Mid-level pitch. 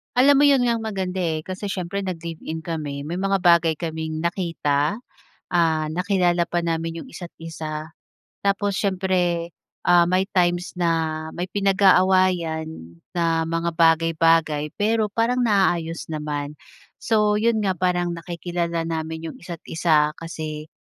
Yes: medium, 170 Hz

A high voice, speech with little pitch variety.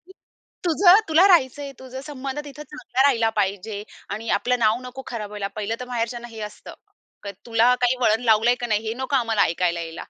No: high, 240 Hz; average, 3.5 semitones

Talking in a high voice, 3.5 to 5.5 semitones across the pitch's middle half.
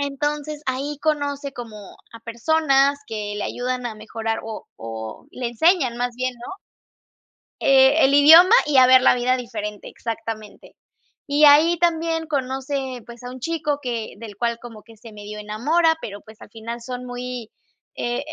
Yes: very high, 250 Hz; average, 4.0 semitones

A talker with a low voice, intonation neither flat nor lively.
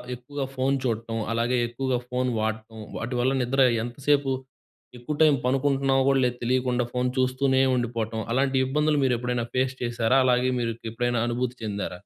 No: low, 125 Hz; narrow, 2.0 semitones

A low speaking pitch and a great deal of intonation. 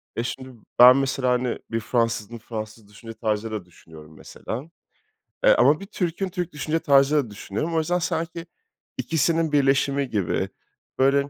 Yes: low, 130 Hz; wide, 5.9 semitones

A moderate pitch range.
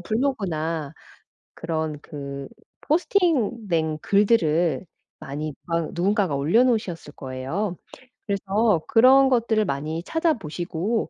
No: wide, 6.4 semitones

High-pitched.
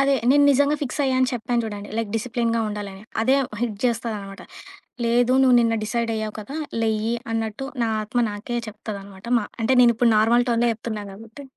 Yes: high, 230 Hz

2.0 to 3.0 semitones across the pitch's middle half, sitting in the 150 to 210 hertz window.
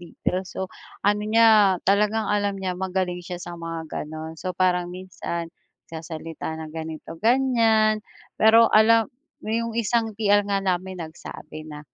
No: average, 4.3 semitones; high, 190 Hz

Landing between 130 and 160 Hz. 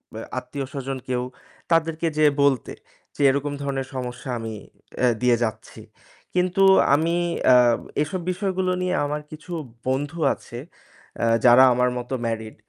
Yes: medium, 140 Hz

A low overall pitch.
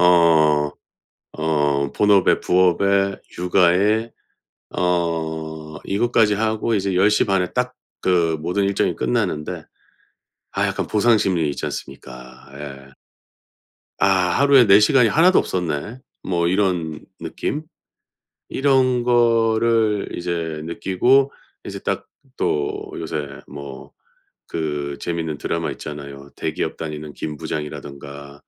Yes: very low, 90 Hz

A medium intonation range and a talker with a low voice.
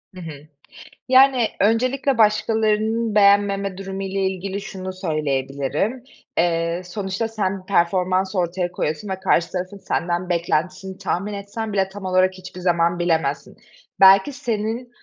No: average, 3.0 semitones; high, 190 Hz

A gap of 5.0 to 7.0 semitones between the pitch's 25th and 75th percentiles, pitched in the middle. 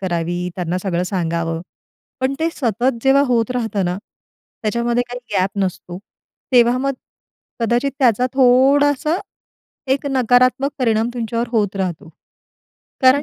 No: wide, 5.4 semitones; high, 235 Hz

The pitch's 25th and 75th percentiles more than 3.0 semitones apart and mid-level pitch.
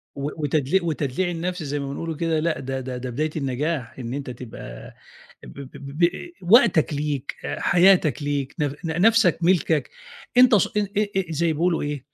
Yes: average, 4.1 semitones; medium, 155 Hz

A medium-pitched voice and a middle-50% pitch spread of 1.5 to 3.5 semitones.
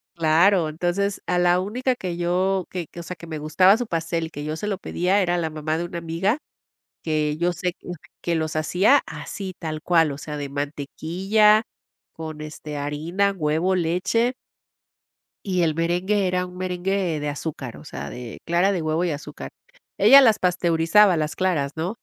Yes: medium, 175 Hz; average, 3.2 semitones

